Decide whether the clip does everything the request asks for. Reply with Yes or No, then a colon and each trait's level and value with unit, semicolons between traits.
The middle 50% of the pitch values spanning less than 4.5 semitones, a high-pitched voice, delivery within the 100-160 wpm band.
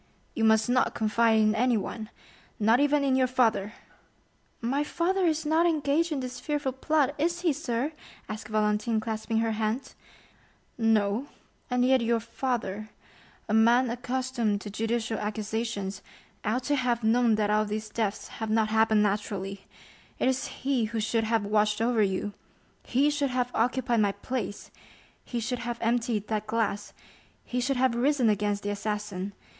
Yes: average, 3.1 semitones; high, 230 Hz; average, 150 wpm